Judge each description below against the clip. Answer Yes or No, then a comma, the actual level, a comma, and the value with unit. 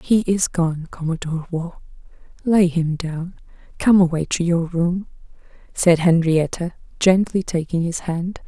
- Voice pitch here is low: No, medium, 170 Hz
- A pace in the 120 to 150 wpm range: Yes, slow, 135 wpm